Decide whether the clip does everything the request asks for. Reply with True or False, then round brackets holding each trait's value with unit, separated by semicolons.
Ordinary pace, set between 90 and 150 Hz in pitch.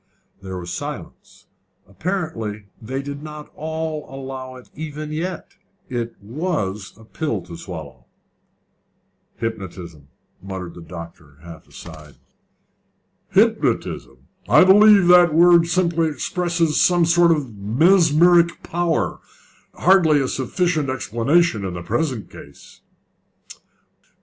False (110 wpm; 140 Hz)